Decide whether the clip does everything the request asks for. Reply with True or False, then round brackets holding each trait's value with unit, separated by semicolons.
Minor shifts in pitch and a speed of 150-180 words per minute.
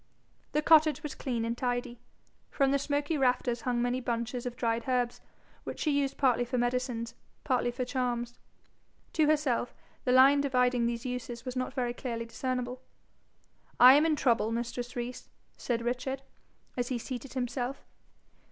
True (1.8 semitones; 160 wpm)